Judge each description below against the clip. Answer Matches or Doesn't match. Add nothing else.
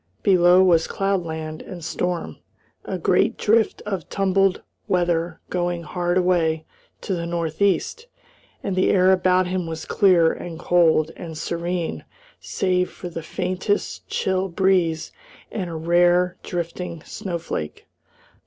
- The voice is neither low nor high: Matches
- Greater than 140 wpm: Doesn't match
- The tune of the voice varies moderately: Doesn't match